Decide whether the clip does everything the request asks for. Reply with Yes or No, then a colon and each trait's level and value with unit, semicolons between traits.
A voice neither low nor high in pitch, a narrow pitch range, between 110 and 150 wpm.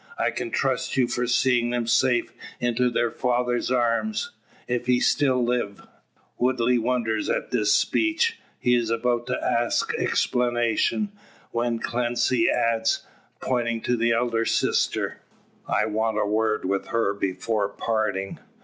No: low, 120 Hz; narrow, 1.5 semitones; average, 140 wpm